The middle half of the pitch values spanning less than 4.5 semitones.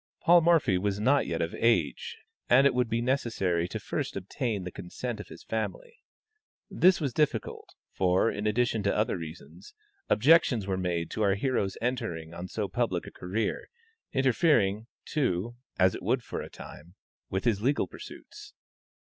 No: wide, 5.4 semitones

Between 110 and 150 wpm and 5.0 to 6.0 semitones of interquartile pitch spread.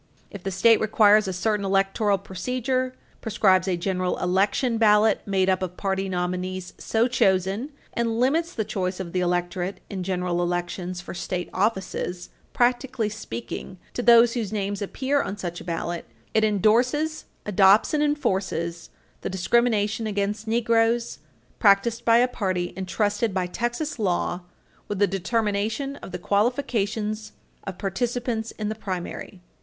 No: average, 145 wpm; average, 3.7 semitones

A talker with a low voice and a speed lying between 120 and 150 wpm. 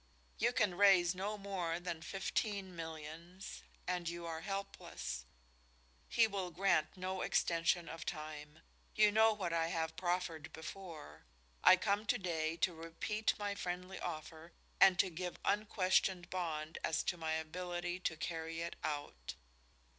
No: medium, 175 Hz; average, 145 wpm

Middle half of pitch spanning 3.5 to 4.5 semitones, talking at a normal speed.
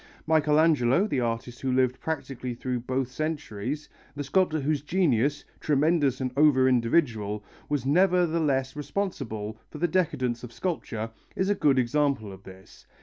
Yes: average, 4.2 semitones; average, 145 wpm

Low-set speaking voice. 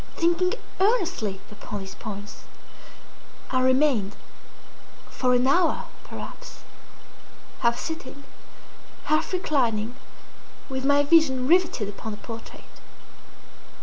No: very high, 260 Hz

